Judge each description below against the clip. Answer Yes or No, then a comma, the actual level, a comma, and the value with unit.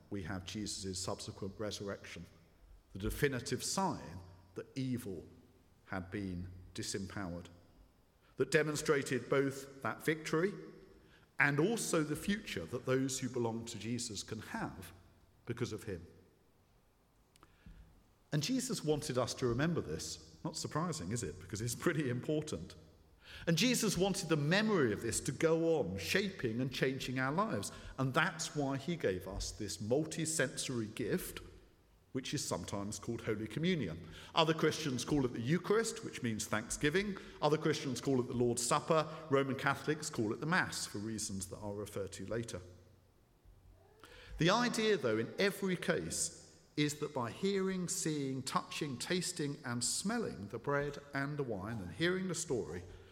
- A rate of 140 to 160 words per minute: Yes, average, 150 wpm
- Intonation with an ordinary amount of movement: No, wide, 8.0 semitones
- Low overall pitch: Yes, low, 120 Hz